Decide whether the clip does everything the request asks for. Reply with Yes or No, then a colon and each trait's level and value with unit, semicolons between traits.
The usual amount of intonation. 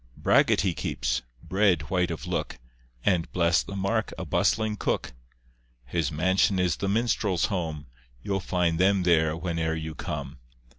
Yes: average, 3.2 semitones